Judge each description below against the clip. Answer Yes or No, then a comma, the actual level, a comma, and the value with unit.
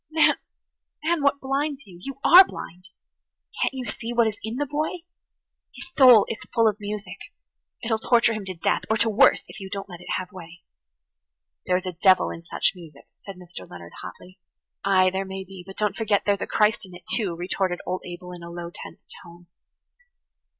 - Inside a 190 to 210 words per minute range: Yes, average, 200 wpm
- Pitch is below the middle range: No, high, 195 Hz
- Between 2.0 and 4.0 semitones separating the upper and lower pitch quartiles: No, average, 4.5 semitones